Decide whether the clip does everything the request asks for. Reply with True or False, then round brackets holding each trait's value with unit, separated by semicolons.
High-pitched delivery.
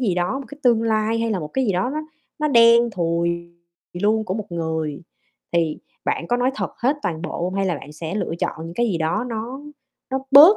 True (210 Hz)